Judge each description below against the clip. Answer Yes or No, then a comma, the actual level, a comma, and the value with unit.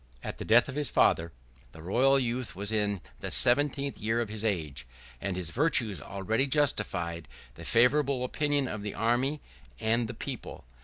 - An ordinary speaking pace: Yes, average, 170 wpm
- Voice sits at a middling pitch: No, low, 115 Hz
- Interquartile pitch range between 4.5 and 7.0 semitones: Yes, average, 5.0 semitones